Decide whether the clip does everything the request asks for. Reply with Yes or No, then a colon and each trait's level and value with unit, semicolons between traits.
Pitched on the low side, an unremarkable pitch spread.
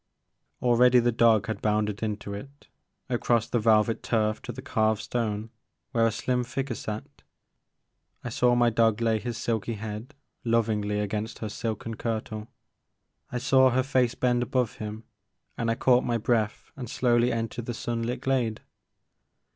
No: low, 115 Hz; narrow, 2.0 semitones